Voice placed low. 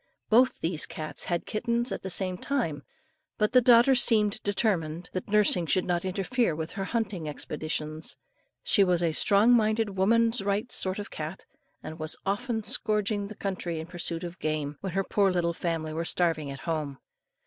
No: high, 190 Hz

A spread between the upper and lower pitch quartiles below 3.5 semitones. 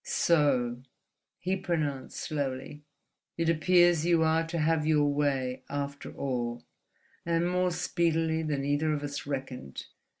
Yes: average, 3.1 semitones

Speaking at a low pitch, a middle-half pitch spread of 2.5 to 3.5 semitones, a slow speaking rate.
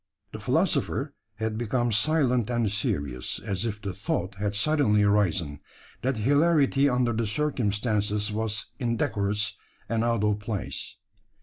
Yes: low, 110 Hz; average, 3.0 semitones; slow, 130 wpm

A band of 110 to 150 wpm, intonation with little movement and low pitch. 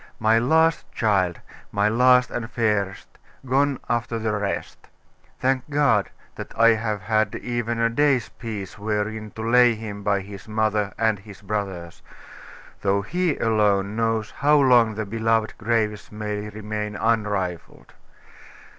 Yes: slow, 135 wpm; narrow, 2.1 semitones; low, 110 Hz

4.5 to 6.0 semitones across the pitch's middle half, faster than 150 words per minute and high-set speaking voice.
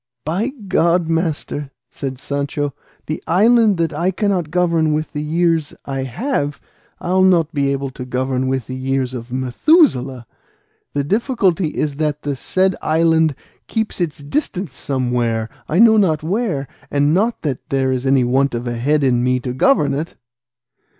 No: average, 5.1 semitones; average, 160 wpm; medium, 150 Hz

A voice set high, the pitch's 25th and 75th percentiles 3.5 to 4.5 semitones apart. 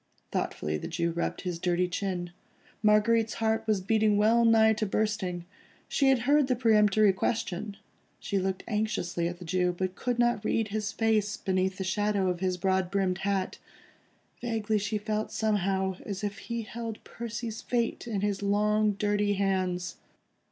No: high, 205 Hz; average, 2.8 semitones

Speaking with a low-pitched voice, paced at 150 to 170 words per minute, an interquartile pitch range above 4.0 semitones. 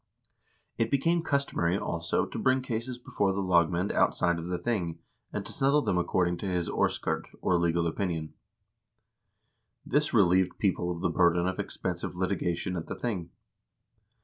Yes: very low, 90 Hz; average, 155 wpm; average, 4.4 semitones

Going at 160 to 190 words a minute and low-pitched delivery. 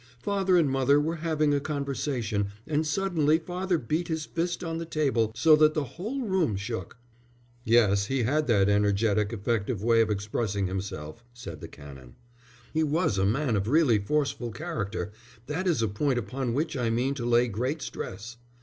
Yes: average, 175 wpm; low, 130 Hz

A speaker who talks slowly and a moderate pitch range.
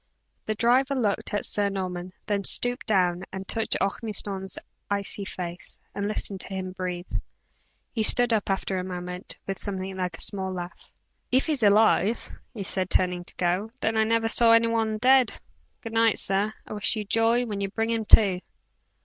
No: average, 190 wpm; average, 3.2 semitones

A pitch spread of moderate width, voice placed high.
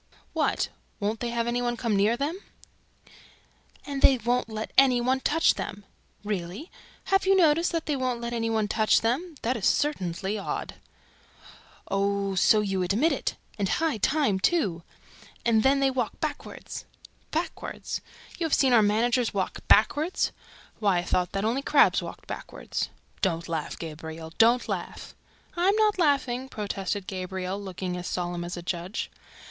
No: wide, 5.8 semitones; high, 225 Hz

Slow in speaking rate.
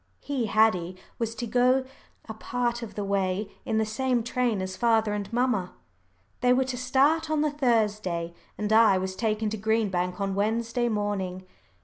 No: average, 175 wpm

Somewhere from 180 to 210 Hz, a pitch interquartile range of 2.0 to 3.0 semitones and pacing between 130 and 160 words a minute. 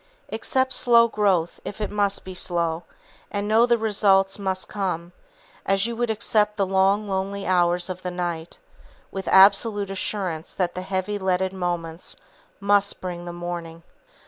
Yes: high, 190 Hz; narrow, 2.6 semitones; average, 155 wpm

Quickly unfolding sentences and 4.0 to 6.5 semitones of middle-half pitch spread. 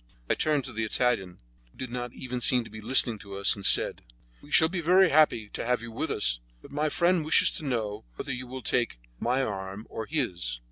Yes: fast, 230 wpm; average, 5.3 semitones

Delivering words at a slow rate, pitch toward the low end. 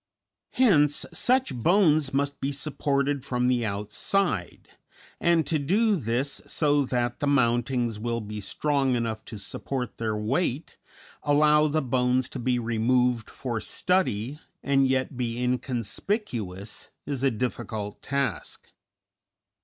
Yes: slow, 125 wpm; low, 130 Hz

